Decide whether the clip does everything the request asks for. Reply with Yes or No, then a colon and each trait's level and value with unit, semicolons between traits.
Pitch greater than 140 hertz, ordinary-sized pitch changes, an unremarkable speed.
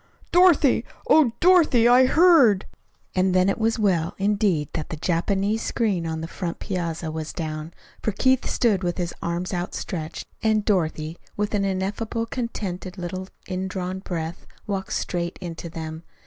Yes: high, 190 Hz; average, 4.4 semitones; average, 150 wpm